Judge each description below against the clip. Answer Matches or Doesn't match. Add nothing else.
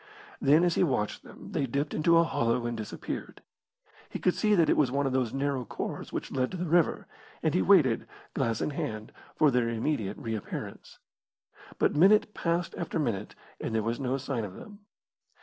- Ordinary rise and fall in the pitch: Doesn't match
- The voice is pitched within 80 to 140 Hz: Matches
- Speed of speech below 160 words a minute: Doesn't match